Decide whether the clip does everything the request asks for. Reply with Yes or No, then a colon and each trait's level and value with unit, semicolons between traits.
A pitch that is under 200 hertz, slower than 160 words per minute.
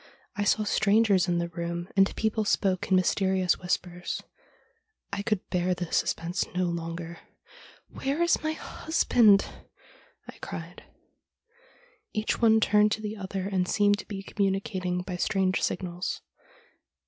Yes: high, 190 Hz; average, 145 wpm